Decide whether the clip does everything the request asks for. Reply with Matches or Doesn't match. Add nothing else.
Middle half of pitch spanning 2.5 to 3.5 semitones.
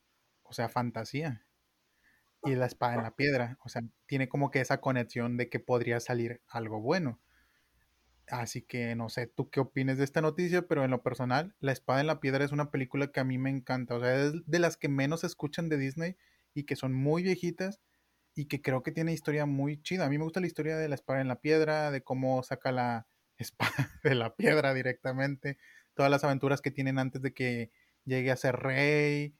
Matches